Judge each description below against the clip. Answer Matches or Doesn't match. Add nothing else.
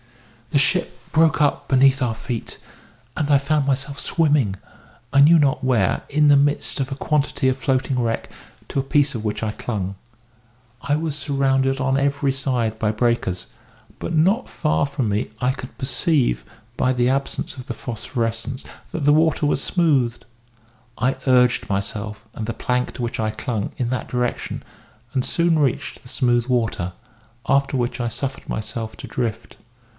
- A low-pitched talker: Matches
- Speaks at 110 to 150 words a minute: Doesn't match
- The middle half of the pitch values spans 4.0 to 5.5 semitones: Doesn't match